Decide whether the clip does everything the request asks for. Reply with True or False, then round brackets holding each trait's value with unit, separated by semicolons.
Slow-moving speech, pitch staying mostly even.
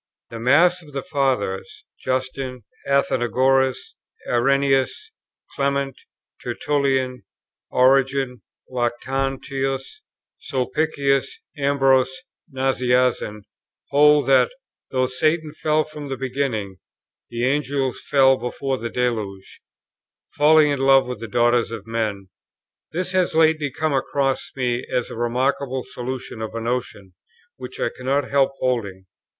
True (110 wpm; 2.2 semitones)